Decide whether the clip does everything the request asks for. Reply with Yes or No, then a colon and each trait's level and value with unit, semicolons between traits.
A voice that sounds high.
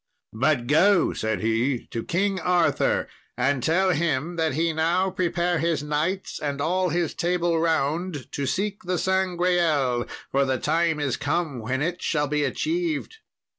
No: medium, 165 Hz